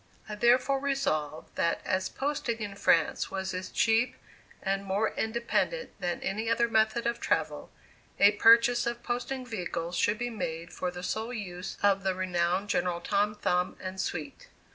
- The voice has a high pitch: Yes, high, 205 Hz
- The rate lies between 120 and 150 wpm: No, average, 165 wpm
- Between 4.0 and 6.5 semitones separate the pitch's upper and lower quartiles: Yes, average, 4.5 semitones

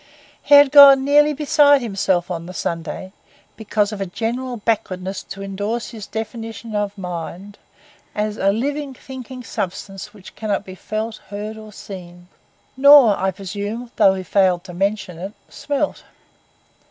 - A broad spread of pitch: No, average, 4.2 semitones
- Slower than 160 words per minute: Yes, average, 145 wpm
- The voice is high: Yes, high, 210 Hz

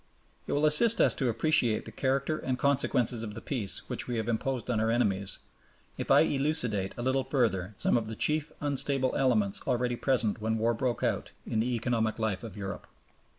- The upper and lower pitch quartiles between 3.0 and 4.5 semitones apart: Yes, average, 3.5 semitones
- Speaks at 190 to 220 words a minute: Yes, average, 195 wpm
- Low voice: Yes, low, 120 Hz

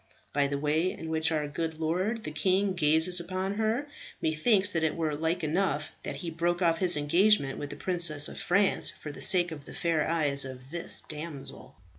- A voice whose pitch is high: No, medium, 165 Hz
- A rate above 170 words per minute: Yes, average, 200 wpm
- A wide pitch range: No, average, 3.4 semitones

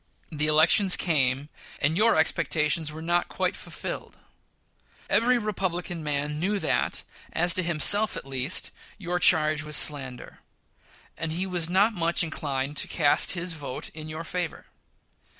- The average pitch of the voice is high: No, medium, 160 Hz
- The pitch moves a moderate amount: Yes, average, 3.0 semitones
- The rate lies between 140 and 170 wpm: Yes, average, 155 wpm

